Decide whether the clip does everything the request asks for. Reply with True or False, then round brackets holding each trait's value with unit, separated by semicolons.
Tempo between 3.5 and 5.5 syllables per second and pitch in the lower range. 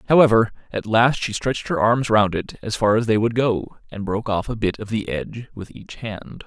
True (5.3 syllables/s; 110 Hz)